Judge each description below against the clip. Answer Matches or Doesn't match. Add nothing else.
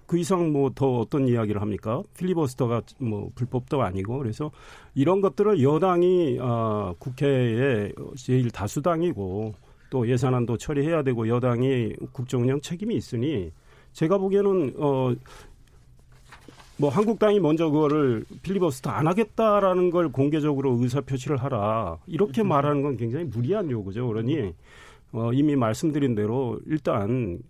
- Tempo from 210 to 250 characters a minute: Doesn't match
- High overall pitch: Doesn't match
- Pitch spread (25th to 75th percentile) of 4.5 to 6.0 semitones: Matches